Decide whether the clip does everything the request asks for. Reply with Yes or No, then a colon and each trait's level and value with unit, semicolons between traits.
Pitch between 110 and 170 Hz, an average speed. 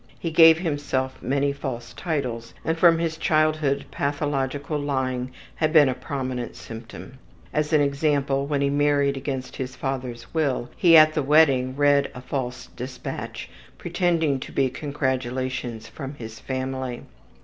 Yes: medium, 140 Hz; average, 150 wpm